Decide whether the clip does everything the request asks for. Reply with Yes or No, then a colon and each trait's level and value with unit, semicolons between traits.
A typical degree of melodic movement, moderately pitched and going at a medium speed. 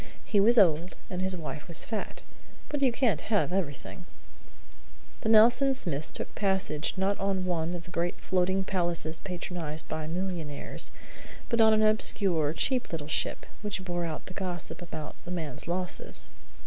Yes: average, 3.4 semitones; medium, 180 Hz; average, 160 wpm